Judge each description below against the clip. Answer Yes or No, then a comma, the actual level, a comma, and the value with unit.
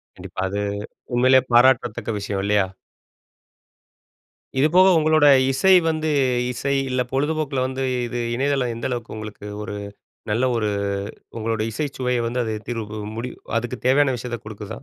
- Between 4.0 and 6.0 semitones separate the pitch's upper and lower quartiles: No, average, 3.3 semitones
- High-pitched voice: No, low, 125 Hz